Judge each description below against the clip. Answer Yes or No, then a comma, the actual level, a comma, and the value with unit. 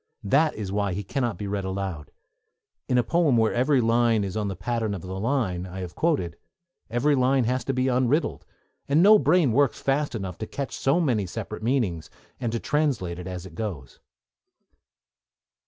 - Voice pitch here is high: No, low, 115 Hz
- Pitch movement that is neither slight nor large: No, wide, 6.0 semitones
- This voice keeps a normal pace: Yes, average, 185 wpm